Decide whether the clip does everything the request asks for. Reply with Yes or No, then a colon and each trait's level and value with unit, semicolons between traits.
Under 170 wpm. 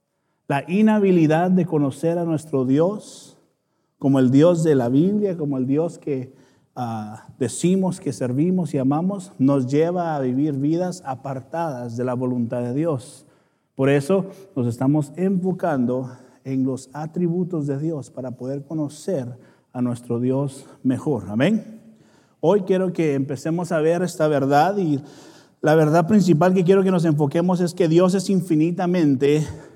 Yes: average, 150 wpm